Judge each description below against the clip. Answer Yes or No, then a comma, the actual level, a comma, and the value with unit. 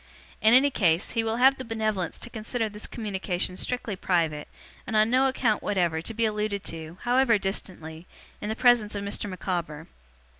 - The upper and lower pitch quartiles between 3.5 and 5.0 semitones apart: Yes, average, 4.2 semitones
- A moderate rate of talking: Yes, average, 180 wpm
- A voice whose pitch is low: No, high, 210 Hz